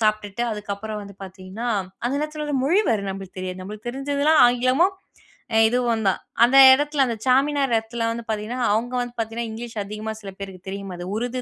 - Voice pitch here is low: No, high, 230 Hz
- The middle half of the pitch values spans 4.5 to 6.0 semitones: No, average, 3.7 semitones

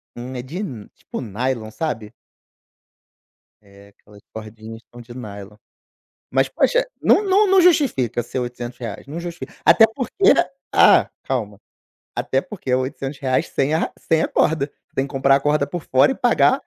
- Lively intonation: Yes, wide, 6.1 semitones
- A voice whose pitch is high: No, low, 130 Hz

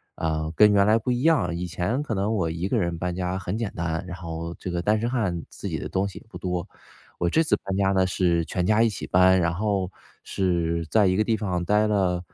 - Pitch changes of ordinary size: Yes, average, 3.4 semitones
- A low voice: Yes, very low, 95 Hz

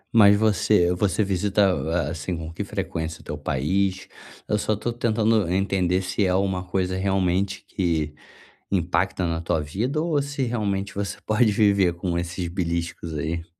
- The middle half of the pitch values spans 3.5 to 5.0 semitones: No, average, 3.1 semitones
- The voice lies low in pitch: Yes, very low, 95 Hz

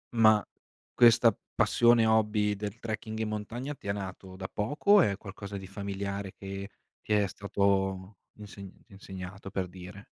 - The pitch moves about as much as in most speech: No, narrow, 2.1 semitones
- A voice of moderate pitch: No, low, 100 Hz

